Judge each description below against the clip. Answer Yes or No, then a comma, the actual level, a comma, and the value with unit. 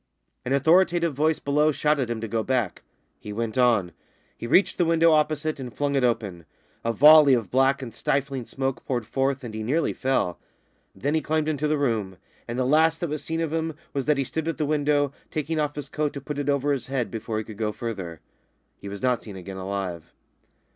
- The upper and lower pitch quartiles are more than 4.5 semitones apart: Yes, average, 4.9 semitones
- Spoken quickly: Yes, fast, 225 wpm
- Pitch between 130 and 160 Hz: Yes, low, 135 Hz